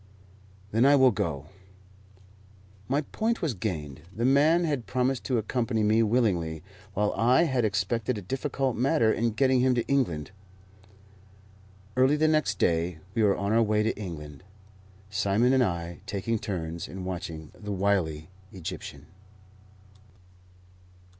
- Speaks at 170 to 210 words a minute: No, average, 140 wpm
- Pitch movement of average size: No, wide, 6.1 semitones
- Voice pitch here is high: No, low, 110 Hz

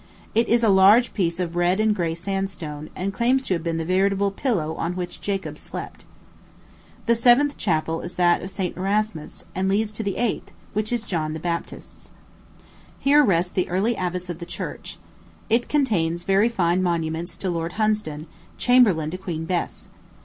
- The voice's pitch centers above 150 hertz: Yes, medium, 185 Hz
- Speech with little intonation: No, average, 4.0 semitones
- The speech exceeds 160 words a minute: Yes, average, 180 wpm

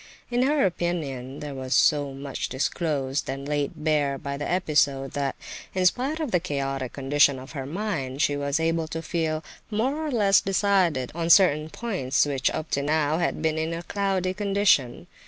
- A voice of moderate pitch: Yes, medium, 155 Hz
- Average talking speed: Yes, average, 180 wpm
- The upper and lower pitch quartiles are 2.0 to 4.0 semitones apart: No, average, 4.9 semitones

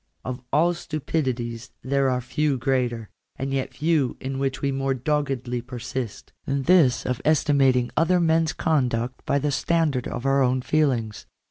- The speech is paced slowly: No, average, 160 wpm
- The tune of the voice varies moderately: Yes, average, 3.0 semitones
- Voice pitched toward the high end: No, low, 135 Hz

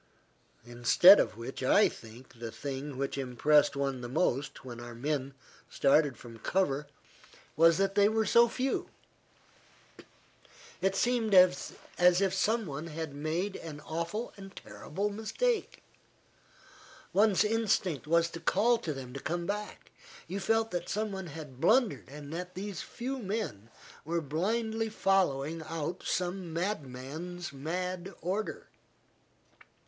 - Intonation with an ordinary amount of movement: No, wide, 6.2 semitones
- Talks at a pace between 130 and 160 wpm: Yes, slow, 135 wpm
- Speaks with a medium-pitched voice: Yes, medium, 170 Hz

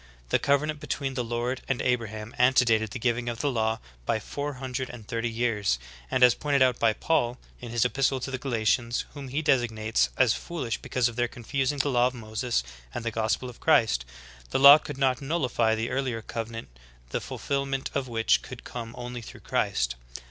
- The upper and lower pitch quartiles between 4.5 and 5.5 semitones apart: No, average, 2.7 semitones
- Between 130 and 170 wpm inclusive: No, average, 200 wpm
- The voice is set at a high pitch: No, low, 120 Hz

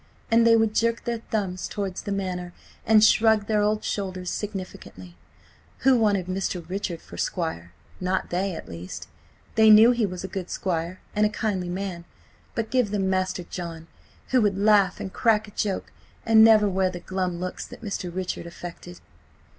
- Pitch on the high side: Yes, high, 195 Hz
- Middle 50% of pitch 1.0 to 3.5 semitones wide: Yes, average, 3.0 semitones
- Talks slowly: No, average, 180 wpm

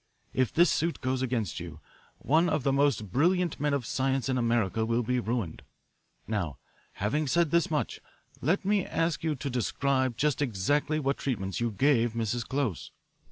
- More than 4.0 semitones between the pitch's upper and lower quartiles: Yes, average, 4.5 semitones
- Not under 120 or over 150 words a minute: No, average, 170 wpm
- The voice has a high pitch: No, low, 130 Hz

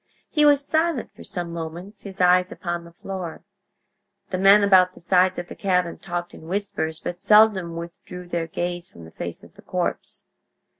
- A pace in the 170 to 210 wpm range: Yes, average, 185 wpm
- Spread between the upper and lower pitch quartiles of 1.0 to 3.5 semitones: Yes, narrow, 2.5 semitones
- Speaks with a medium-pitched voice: Yes, medium, 180 Hz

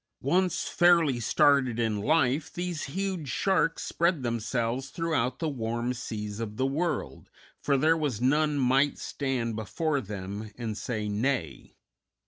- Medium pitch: No, low, 130 Hz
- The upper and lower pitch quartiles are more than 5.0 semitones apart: Yes, wide, 5.5 semitones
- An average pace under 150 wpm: Yes, slow, 135 wpm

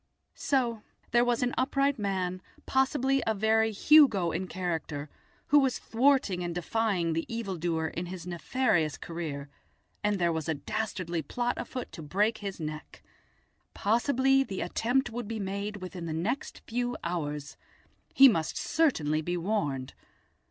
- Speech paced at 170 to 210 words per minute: No, average, 145 wpm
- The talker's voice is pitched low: No, high, 200 Hz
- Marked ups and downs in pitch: Yes, wide, 6.4 semitones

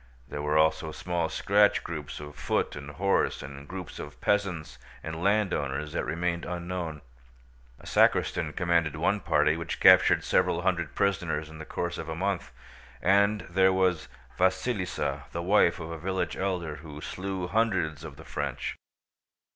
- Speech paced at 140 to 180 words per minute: Yes, average, 155 wpm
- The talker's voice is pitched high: No, very low, 85 Hz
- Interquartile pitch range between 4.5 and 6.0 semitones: No, average, 3.6 semitones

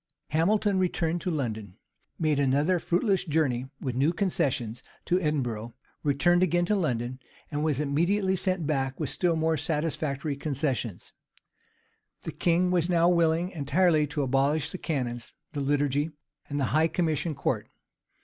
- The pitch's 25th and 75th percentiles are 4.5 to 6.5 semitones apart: No, average, 4.1 semitones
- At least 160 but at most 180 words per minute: No, average, 150 wpm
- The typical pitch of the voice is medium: Yes, medium, 155 Hz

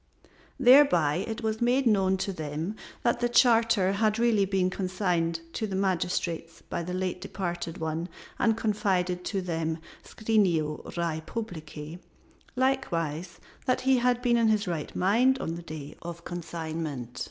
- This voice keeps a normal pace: Yes, average, 155 wpm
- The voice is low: No, medium, 185 Hz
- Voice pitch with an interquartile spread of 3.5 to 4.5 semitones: No, average, 5.2 semitones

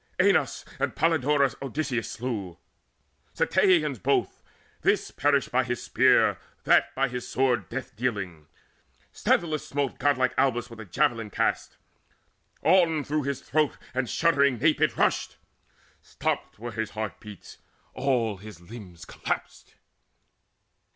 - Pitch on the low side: Yes, low, 130 Hz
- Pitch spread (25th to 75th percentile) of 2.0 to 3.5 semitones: No, average, 4.4 semitones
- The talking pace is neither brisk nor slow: No, slow, 125 wpm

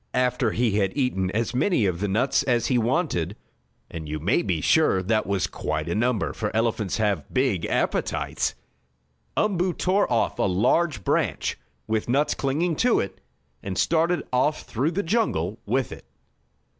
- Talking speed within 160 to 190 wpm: Yes, average, 165 wpm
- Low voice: Yes, low, 115 Hz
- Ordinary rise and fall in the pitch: No, wide, 7.1 semitones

